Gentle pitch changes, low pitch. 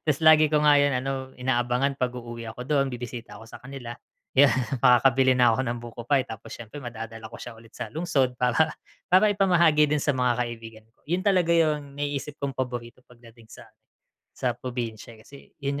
No: average, 3.5 semitones; low, 130 Hz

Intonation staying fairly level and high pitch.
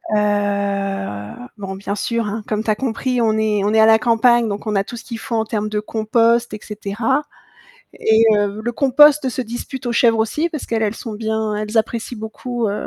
Yes: narrow, 2.1 semitones; high, 220 Hz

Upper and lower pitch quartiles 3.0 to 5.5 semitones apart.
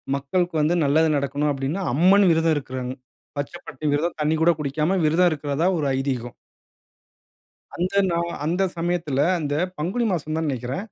Yes: average, 3.5 semitones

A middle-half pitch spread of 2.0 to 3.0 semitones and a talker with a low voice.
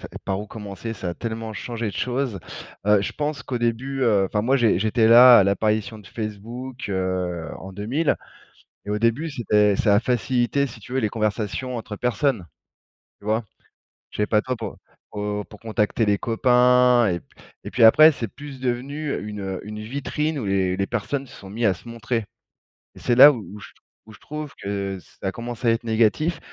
No: average, 3.4 semitones; low, 115 Hz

